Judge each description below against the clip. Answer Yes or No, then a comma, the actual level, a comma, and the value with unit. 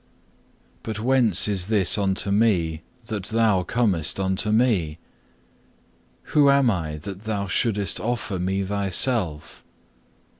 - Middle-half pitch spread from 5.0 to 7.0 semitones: No, average, 3.3 semitones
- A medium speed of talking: No, slow, 115 wpm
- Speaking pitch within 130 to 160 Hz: No, low, 100 Hz